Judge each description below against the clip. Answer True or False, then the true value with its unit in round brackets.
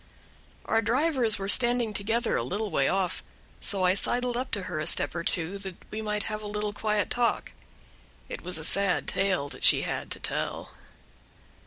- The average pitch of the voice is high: True (210 Hz)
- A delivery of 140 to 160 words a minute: False (190 wpm)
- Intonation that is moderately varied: True (3.3 semitones)